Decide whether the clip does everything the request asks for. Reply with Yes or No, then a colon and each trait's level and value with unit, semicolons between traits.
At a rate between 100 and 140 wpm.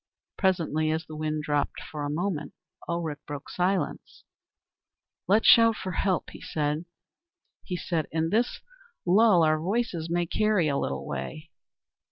Yes: slow, 135 wpm